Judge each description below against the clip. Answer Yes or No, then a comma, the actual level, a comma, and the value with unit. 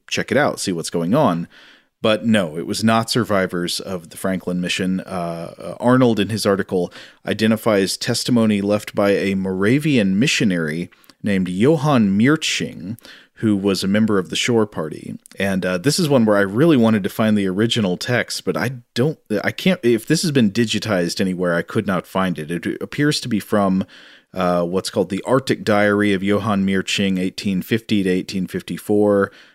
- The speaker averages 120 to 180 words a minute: Yes, average, 175 wpm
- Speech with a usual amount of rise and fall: Yes, average, 3.2 semitones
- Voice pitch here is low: Yes, low, 100 Hz